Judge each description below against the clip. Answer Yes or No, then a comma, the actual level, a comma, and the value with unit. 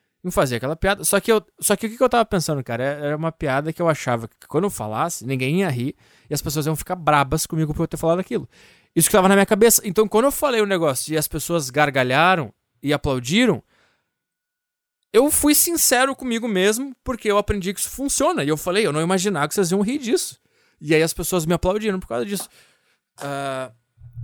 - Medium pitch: Yes, medium, 180 Hz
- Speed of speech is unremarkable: No, fast, 225 wpm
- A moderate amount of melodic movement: No, wide, 6.2 semitones